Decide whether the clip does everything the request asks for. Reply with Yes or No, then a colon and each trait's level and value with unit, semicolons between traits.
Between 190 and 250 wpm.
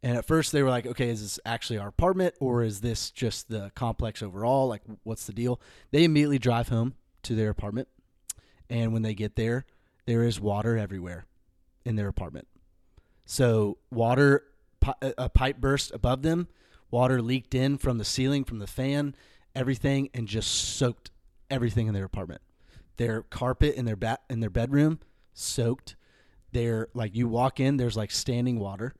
No: average, 175 wpm